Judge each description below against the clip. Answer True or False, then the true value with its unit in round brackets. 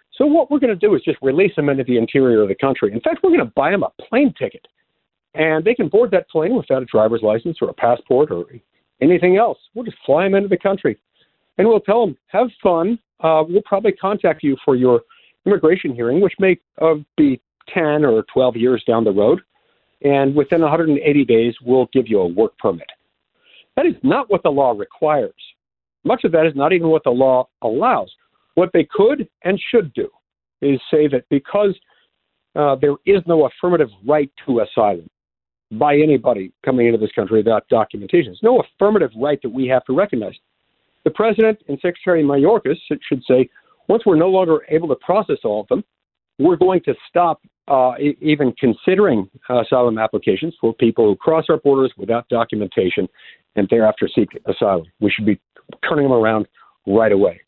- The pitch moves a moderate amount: False (7.6 semitones)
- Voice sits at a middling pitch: True (150 Hz)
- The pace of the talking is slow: False (195 wpm)